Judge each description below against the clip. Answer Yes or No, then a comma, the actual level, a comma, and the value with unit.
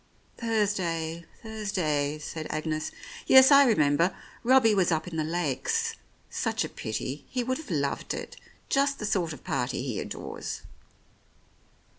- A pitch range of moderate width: No, wide, 6.5 semitones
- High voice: No, medium, 175 Hz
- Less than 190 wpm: Yes, average, 140 wpm